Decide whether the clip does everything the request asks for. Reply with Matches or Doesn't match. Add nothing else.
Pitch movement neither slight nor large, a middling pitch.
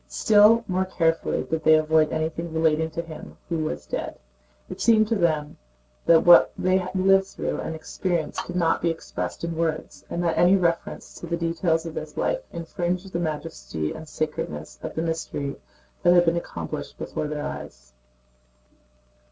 Doesn't match